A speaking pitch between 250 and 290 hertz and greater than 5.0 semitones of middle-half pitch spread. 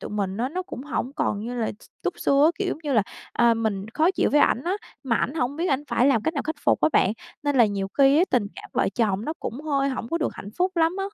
Yes: very high, 270 Hz; wide, 5.5 semitones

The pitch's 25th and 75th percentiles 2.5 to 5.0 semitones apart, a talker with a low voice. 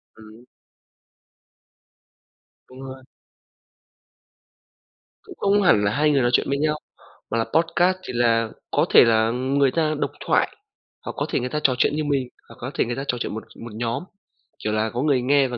Yes: average, 4.1 semitones; low, 130 Hz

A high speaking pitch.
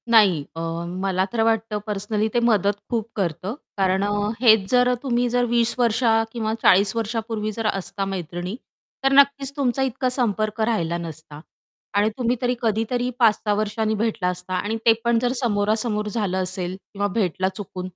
Yes: high, 215 Hz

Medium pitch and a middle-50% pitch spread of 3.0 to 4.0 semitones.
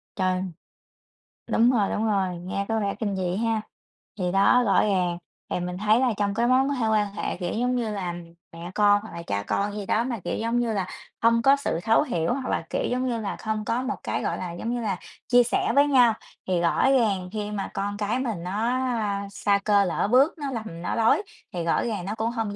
No: high, 215 Hz; average, 3.7 semitones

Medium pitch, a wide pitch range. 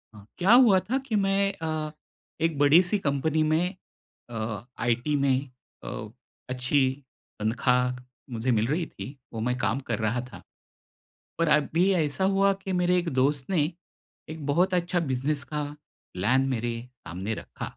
Yes: medium, 145 Hz; wide, 5.9 semitones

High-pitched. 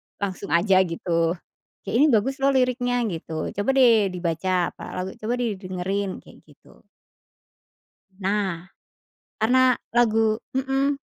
Yes: high, 205 Hz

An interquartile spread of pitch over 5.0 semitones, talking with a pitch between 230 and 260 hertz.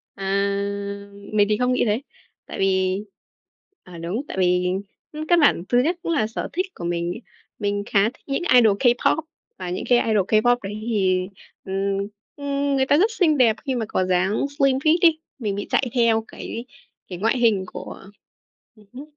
No: wide, 5.5 semitones; high, 220 Hz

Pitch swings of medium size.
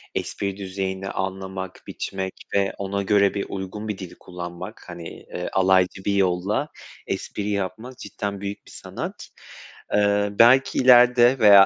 No: narrow, 1.6 semitones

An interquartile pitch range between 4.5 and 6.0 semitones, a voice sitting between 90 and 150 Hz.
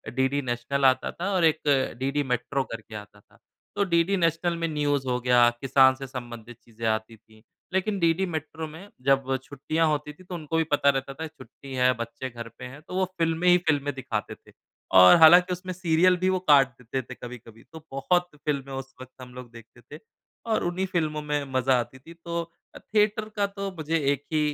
Yes: average, 4.8 semitones; medium, 140 Hz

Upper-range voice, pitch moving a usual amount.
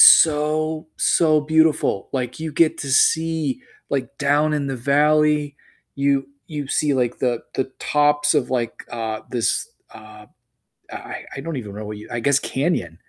No: medium, 140 Hz; average, 3.5 semitones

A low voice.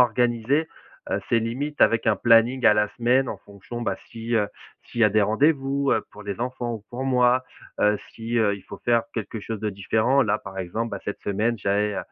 Yes: low, 115 Hz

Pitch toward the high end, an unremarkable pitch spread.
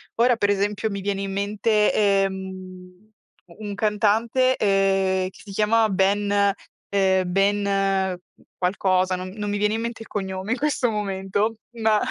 No: high, 200 Hz; narrow, 1.9 semitones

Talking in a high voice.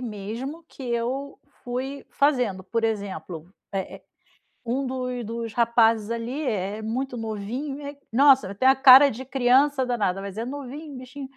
Yes: high, 245 Hz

